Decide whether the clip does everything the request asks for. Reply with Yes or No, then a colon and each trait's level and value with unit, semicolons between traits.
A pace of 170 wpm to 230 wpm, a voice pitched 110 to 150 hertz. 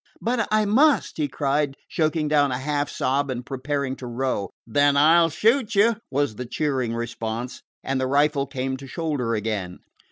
Yes: average, 180 wpm; medium, 140 Hz